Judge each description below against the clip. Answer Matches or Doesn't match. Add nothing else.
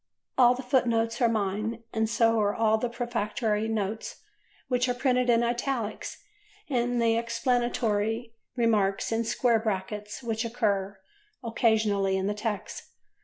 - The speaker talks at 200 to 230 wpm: Doesn't match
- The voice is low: Doesn't match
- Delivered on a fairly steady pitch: Matches